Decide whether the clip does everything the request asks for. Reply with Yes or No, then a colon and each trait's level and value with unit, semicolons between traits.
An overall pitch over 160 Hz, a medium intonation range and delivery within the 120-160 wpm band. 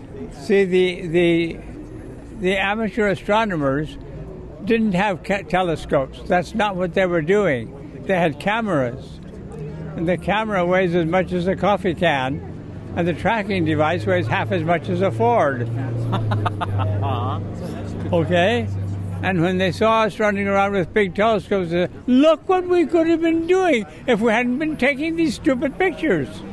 No: medium, 185 Hz; wide, 5.9 semitones; average, 155 wpm